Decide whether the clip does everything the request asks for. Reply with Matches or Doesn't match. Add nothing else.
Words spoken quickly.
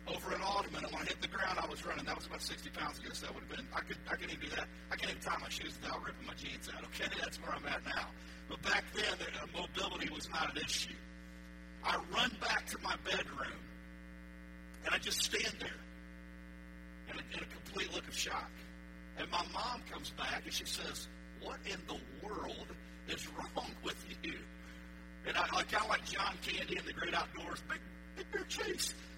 Matches